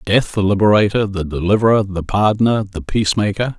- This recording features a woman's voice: No, male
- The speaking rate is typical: Yes, average, 165 wpm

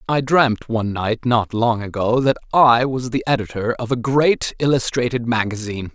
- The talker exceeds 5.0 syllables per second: No, 4.9 syllables/s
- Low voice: Yes, low, 120 Hz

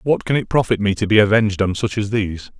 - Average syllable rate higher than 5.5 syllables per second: Yes, 6.5 syllables/s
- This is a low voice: Yes, low, 105 Hz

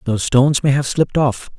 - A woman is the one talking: No, male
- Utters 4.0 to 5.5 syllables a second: No, 6.5 syllables/s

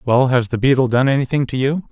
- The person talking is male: Yes, male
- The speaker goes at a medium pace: No, fast, 250 wpm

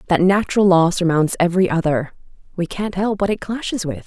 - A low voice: No, medium, 185 Hz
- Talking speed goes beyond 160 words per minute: Yes, average, 190 wpm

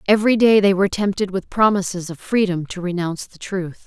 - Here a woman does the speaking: Yes, female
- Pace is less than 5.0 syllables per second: No, 5.9 syllables/s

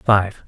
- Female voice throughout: No, male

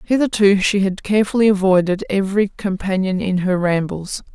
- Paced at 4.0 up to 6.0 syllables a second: Yes, 5.4 syllables/s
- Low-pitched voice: No, high, 195 Hz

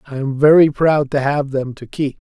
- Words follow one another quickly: Yes, fast, 240 wpm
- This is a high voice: No, medium, 140 Hz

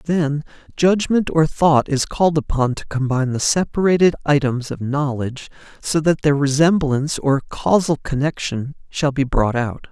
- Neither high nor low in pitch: Yes, medium, 145 Hz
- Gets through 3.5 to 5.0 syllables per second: Yes, 4.8 syllables/s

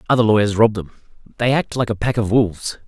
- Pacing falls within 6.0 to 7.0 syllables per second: Yes, 6.5 syllables/s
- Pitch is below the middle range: Yes, low, 110 Hz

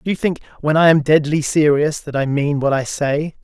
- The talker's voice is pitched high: No, medium, 150 Hz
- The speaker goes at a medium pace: No, fast, 245 wpm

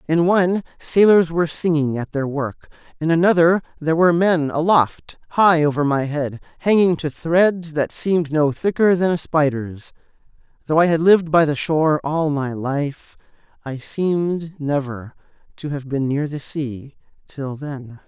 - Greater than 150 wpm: Yes, average, 165 wpm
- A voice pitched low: No, medium, 155 Hz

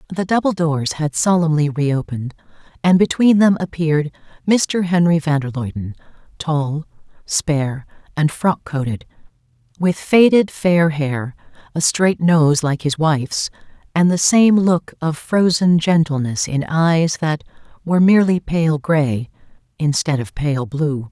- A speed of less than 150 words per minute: Yes, slow, 135 wpm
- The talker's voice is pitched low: No, medium, 160 Hz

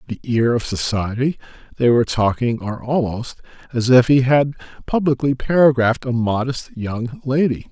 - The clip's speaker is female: No, male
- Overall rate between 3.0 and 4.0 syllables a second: No, 4.9 syllables/s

